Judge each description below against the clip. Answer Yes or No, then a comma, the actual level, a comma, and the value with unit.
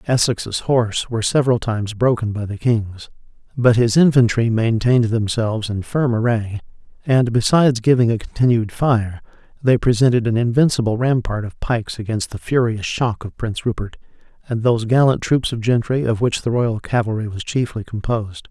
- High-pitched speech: No, low, 115 Hz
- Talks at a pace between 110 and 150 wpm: No, average, 165 wpm